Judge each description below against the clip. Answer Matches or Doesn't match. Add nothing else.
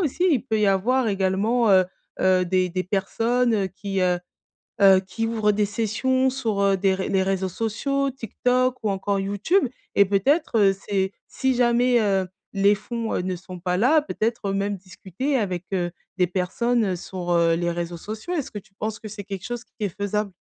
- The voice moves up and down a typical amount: Matches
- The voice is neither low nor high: Doesn't match